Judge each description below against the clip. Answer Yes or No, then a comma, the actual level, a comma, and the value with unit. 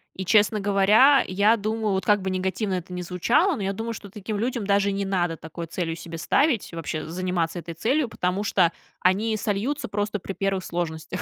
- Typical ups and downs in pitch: Yes, average, 3.1 semitones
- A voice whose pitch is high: Yes, high, 195 Hz